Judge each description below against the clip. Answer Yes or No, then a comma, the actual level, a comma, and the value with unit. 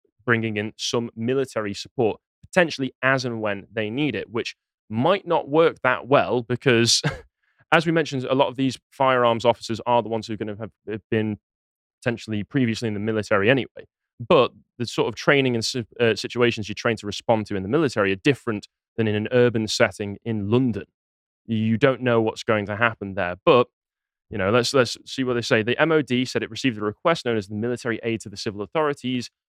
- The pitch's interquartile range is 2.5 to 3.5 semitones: Yes, average, 2.9 semitones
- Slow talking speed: No, fast, 205 wpm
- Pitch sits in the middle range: No, low, 115 Hz